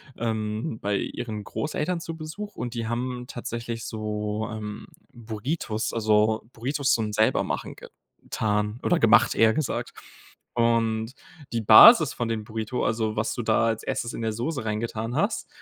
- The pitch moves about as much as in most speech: No, narrow, 2.2 semitones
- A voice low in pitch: Yes, low, 115 Hz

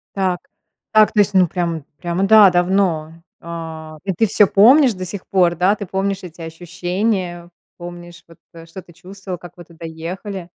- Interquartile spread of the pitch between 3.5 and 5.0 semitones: No, narrow, 2.4 semitones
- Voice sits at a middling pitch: Yes, medium, 180 Hz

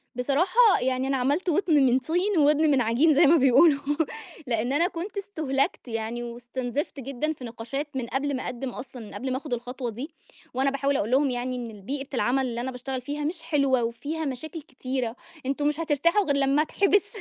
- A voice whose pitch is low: No, very high, 270 Hz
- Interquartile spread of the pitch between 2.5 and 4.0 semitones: Yes, average, 3.5 semitones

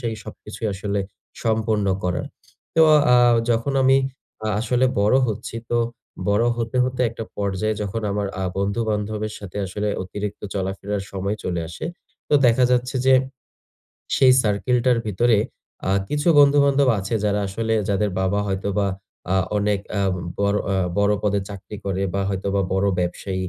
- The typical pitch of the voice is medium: No, low, 105 Hz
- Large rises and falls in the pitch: No, average, 2.8 semitones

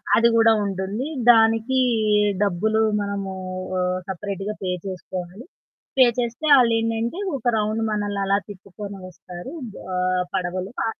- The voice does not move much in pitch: No, average, 3.3 semitones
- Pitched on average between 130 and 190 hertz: No, high, 205 Hz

